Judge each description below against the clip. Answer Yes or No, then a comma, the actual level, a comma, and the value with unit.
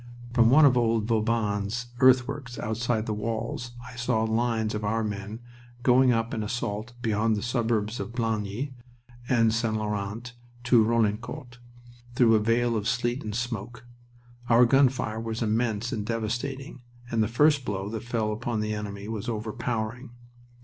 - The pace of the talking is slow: No, average, 155 wpm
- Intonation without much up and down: Yes, narrow, 2.1 semitones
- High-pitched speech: No, low, 115 Hz